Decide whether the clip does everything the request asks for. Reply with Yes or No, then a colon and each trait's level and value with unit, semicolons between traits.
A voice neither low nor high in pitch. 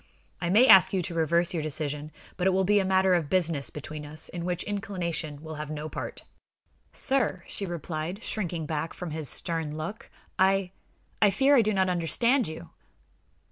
Yes: medium, 175 Hz